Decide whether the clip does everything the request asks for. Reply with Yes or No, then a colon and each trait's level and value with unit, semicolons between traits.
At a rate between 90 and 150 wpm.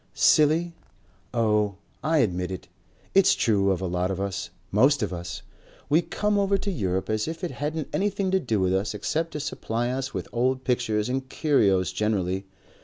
No: average, 180 wpm